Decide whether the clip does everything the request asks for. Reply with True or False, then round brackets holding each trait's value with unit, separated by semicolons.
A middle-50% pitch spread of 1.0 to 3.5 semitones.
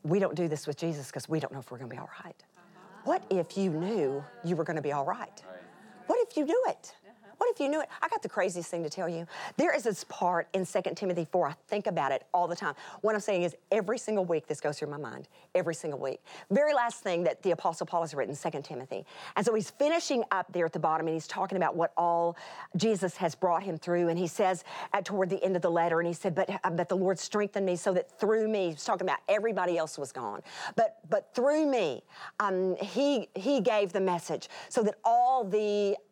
False (3.9 semitones)